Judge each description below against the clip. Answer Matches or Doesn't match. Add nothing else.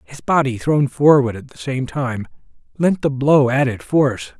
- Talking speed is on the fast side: Doesn't match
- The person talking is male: Matches